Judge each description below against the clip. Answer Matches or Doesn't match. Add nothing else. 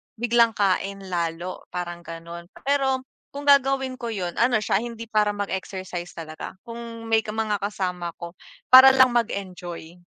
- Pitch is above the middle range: Matches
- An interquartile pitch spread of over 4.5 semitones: Matches